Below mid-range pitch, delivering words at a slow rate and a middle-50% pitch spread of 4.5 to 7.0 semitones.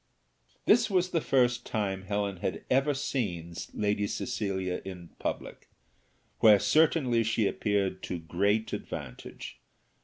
Yes: low, 105 Hz; slow, 120 wpm; average, 4.8 semitones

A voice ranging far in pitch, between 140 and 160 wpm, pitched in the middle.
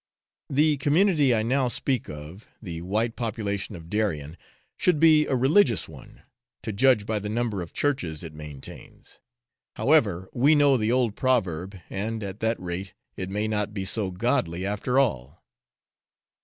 No: wide, 5.7 semitones; average, 155 wpm; low, 110 Hz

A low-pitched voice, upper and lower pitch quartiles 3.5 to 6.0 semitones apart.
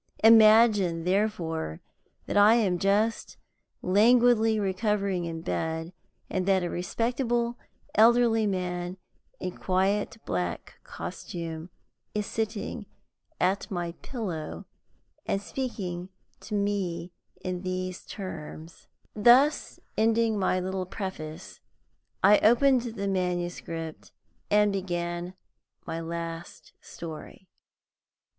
No: high, 190 Hz; average, 3.8 semitones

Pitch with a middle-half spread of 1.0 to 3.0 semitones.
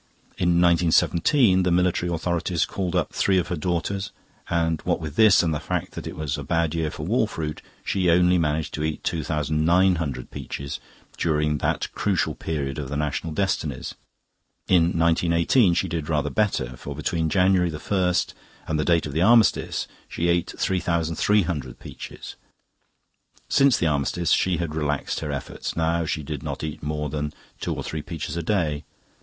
Yes: average, 2.7 semitones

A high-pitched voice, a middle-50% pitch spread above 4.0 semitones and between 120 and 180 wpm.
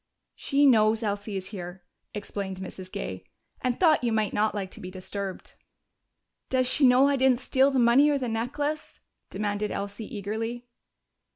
Yes: high, 220 Hz; average, 4.5 semitones; average, 165 wpm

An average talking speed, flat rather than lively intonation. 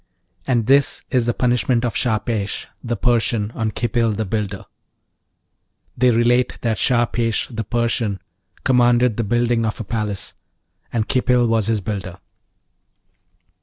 No: slow, 130 wpm; narrow, 2.0 semitones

